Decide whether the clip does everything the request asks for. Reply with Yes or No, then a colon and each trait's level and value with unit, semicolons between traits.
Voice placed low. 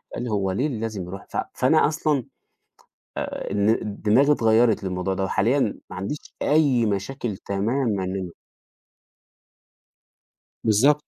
Yes: low, 110 Hz